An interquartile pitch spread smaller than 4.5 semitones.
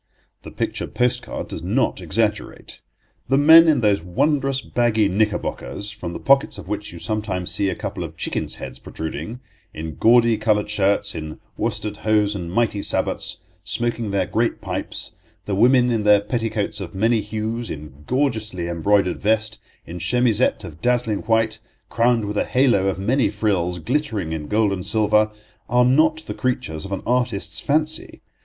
Yes: average, 3.7 semitones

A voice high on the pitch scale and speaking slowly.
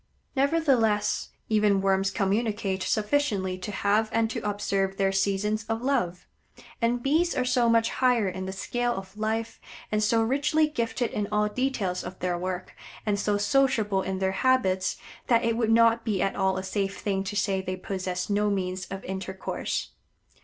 No: high, 210 Hz; average, 175 wpm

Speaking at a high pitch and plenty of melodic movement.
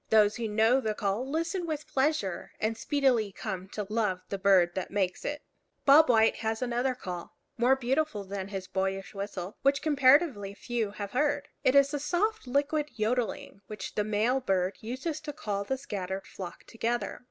Yes: high, 225 Hz; wide, 5.7 semitones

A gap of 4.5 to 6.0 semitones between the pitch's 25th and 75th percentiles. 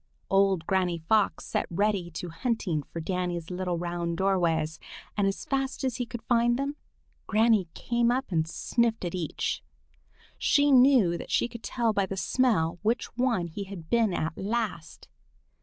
Yes: wide, 5.5 semitones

